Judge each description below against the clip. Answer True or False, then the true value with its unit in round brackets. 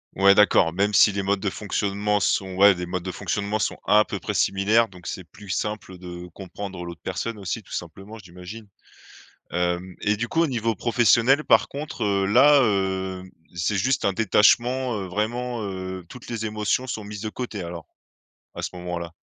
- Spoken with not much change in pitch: False (3.2 semitones)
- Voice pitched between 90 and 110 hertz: True (100 Hz)